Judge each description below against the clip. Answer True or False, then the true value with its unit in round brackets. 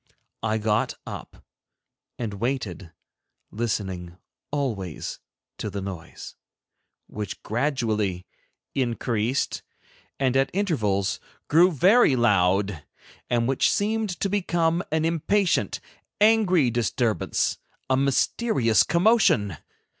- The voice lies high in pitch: False (120 Hz)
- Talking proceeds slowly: True (95 wpm)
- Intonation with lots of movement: True (8.3 semitones)